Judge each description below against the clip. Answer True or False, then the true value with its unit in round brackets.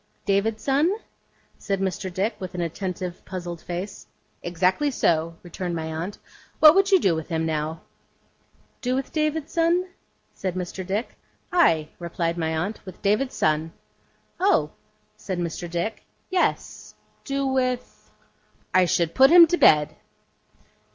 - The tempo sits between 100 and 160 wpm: True (140 wpm)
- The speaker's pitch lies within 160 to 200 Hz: True (185 Hz)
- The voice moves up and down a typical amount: False (7.9 semitones)